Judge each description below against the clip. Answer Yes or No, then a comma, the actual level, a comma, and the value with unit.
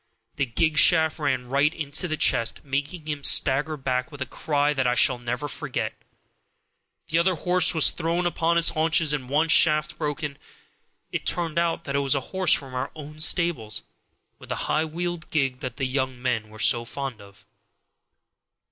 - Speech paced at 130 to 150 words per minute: No, average, 185 wpm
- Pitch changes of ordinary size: Yes, average, 3.7 semitones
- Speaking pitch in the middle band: Yes, medium, 145 Hz